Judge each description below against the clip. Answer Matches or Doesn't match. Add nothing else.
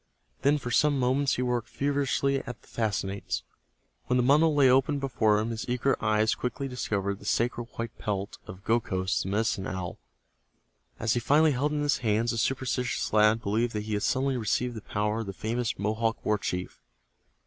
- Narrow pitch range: Doesn't match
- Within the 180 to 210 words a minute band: Matches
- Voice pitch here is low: Matches